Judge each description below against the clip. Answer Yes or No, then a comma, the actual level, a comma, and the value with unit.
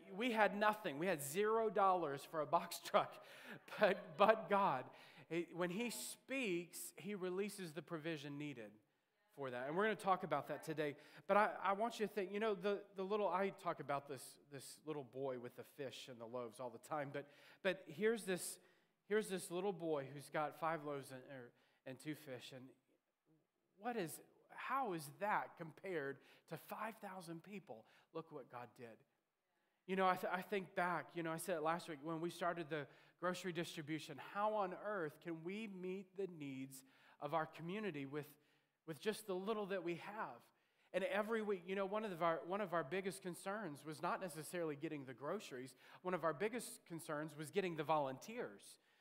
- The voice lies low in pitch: No, medium, 170 Hz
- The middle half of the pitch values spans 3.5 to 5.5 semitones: Yes, average, 4.7 semitones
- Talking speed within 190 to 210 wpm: Yes, average, 195 wpm